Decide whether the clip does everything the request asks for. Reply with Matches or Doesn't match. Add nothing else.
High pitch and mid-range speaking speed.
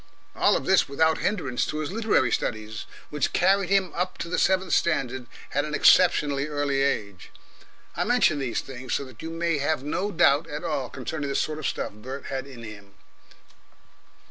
Doesn't match